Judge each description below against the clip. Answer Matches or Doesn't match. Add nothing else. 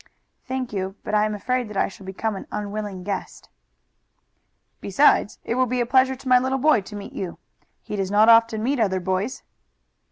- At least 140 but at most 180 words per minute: Doesn't match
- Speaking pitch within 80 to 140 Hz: Doesn't match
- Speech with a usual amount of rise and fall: Matches